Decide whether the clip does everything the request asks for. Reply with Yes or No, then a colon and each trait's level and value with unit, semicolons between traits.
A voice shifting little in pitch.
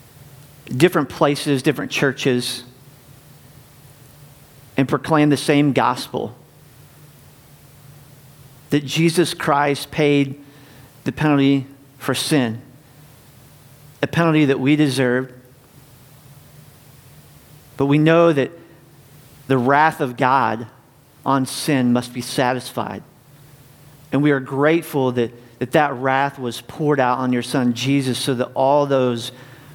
Yes: narrow, 1.6 semitones